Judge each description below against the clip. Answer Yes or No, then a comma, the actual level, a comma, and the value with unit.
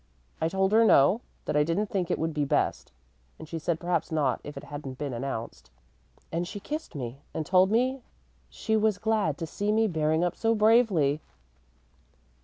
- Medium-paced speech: Yes, average, 190 wpm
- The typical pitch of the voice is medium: Yes, medium, 170 Hz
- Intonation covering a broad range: Yes, wide, 6.2 semitones